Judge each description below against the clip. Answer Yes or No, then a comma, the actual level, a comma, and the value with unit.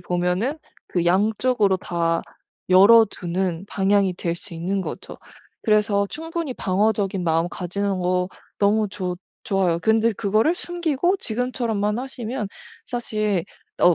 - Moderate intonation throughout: Yes, average, 3.9 semitones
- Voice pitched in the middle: No, high, 200 Hz